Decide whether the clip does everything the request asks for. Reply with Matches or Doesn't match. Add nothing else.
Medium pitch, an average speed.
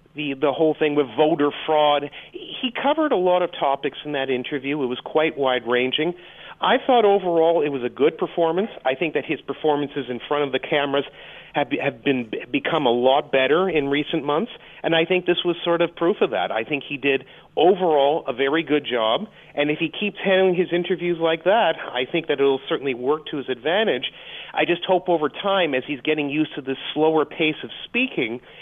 Doesn't match